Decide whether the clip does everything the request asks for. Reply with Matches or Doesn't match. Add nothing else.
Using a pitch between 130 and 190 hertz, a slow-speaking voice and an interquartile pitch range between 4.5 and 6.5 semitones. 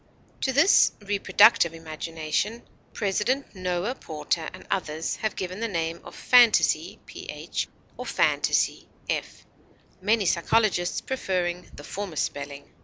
Matches